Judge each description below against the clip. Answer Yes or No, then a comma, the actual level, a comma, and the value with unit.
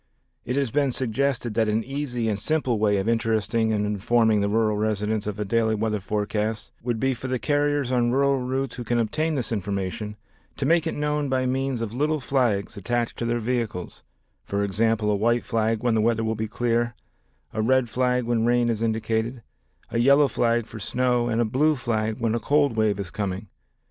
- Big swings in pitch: No, average, 2.8 semitones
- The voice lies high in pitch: No, low, 115 Hz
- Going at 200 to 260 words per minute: Yes, fast, 205 wpm